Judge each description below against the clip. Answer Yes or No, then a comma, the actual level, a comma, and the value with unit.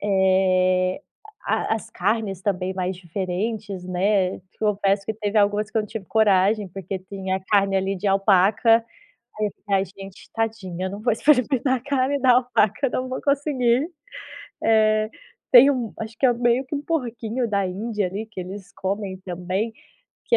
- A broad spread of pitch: No, average, 3.4 semitones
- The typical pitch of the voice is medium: No, high, 205 Hz